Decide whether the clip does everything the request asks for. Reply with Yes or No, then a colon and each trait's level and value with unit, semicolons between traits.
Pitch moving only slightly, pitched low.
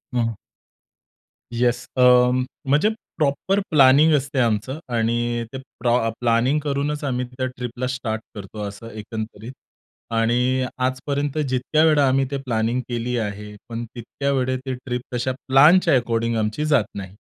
No: average, 3.1 semitones; low, 125 Hz